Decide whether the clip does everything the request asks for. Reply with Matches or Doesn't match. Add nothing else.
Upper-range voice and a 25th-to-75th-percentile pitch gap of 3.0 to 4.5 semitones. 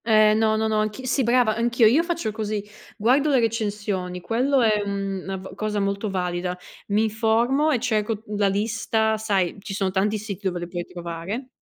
Doesn't match